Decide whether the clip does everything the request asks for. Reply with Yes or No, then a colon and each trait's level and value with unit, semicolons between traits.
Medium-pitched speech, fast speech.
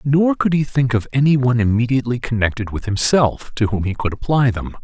No: low, 125 Hz; fast, 210 wpm